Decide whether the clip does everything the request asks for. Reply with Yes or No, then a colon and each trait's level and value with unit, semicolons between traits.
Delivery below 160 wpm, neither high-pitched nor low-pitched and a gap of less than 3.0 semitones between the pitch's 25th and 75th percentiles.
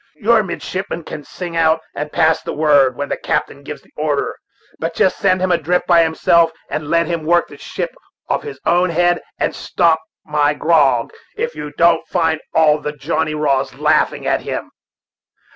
No: average, 180 wpm; medium, 160 Hz; narrow, 2.6 semitones